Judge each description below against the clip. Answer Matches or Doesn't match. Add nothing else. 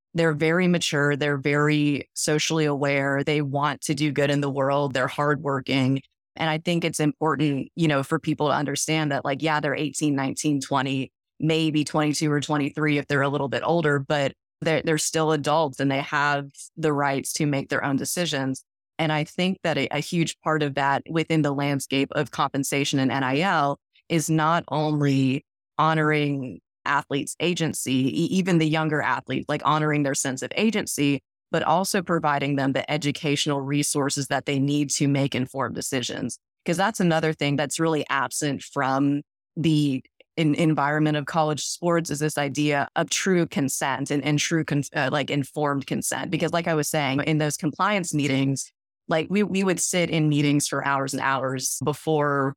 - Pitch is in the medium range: Matches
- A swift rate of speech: Doesn't match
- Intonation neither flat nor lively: Doesn't match